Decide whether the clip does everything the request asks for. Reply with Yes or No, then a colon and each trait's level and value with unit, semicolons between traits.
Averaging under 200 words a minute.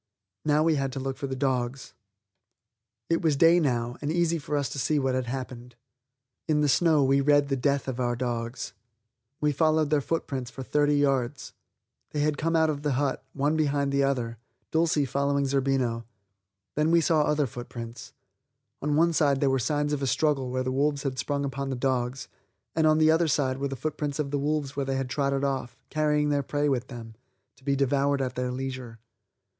No: fast, 205 wpm